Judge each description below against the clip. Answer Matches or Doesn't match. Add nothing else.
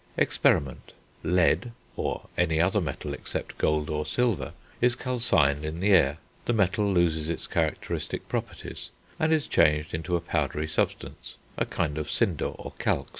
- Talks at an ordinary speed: Matches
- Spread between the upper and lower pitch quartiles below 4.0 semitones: Doesn't match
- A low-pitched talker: Matches